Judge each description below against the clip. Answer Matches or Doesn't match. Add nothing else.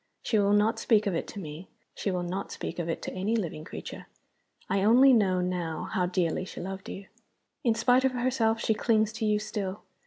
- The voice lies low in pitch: Doesn't match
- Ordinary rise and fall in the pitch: Matches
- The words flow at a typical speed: Doesn't match